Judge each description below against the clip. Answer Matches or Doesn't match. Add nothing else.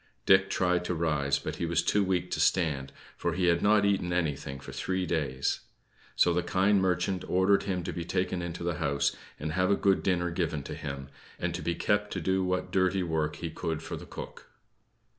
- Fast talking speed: Matches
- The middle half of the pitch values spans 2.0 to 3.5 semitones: Matches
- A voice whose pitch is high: Doesn't match